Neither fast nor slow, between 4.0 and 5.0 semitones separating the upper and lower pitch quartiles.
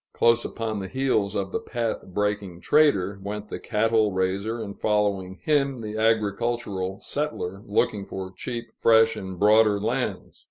No: average, 150 wpm; narrow, 2.6 semitones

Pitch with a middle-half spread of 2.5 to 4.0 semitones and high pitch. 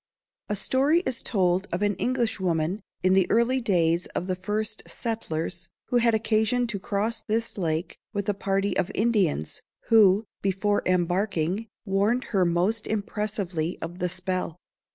Yes: average, 3.5 semitones; high, 200 Hz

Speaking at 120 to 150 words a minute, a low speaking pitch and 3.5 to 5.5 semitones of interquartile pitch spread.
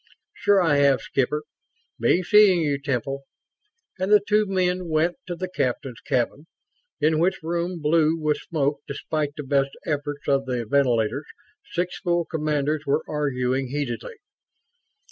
No: average, 145 wpm; medium, 150 Hz; average, 3.8 semitones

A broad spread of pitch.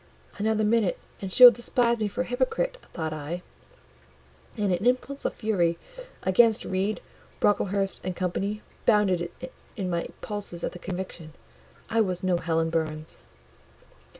No: average, 4.2 semitones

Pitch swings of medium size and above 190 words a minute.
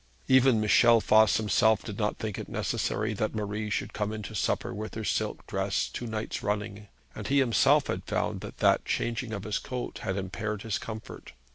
No: narrow, 1.3 semitones; average, 200 wpm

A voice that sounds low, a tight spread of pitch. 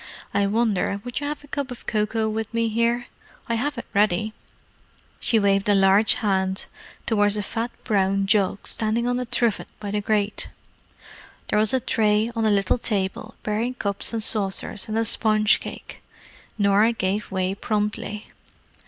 No: high, 215 Hz; narrow, 2.3 semitones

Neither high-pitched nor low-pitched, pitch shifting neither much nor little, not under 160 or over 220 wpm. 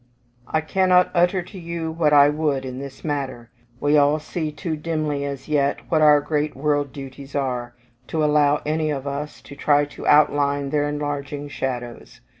No: medium, 145 Hz; narrow, 1.5 semitones; average, 175 wpm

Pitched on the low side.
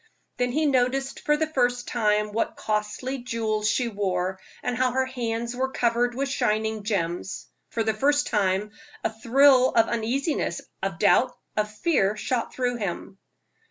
No: high, 235 Hz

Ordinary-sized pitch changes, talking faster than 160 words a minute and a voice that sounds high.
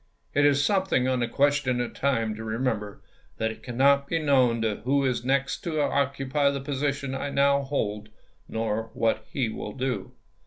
No: average, 3.5 semitones; average, 180 wpm; low, 135 Hz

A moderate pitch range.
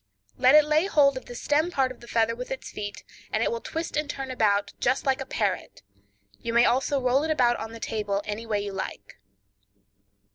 Yes: average, 4.1 semitones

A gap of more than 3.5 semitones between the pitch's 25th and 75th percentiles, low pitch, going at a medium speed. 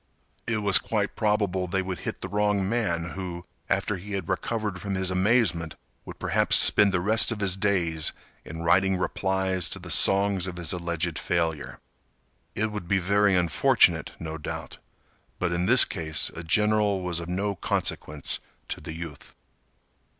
No: average, 2.9 semitones; very low, 95 Hz; average, 165 wpm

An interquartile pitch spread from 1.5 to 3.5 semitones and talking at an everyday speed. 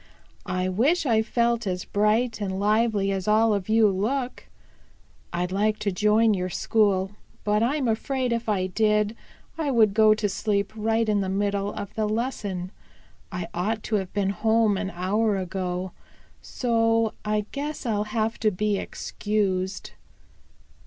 Yes: narrow, 2.5 semitones; average, 155 wpm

